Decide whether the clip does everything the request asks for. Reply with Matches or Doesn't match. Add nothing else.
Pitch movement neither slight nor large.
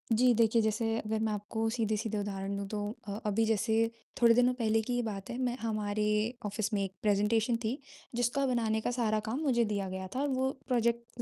Doesn't match